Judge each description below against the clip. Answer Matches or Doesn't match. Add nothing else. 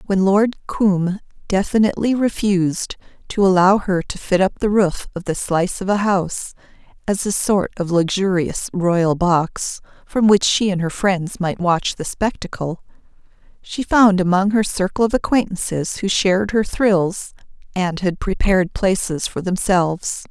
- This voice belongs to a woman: Matches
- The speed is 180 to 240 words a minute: Doesn't match